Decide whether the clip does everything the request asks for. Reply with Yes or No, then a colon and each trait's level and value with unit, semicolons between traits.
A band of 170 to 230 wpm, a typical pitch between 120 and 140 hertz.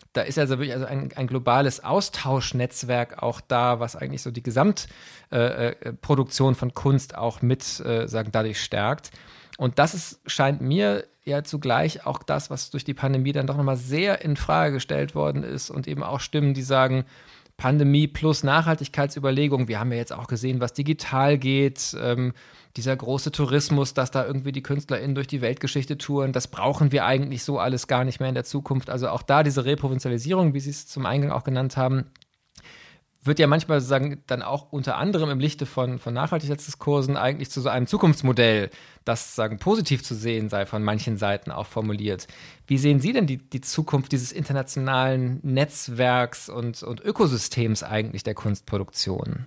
Yes: average, 180 wpm; low, 135 Hz